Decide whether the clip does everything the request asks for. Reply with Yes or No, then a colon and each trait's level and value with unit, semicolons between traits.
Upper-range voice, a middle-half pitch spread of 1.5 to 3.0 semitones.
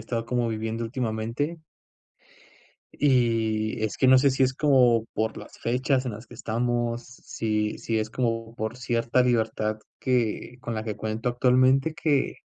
No: low, 120 Hz; narrow, 2.5 semitones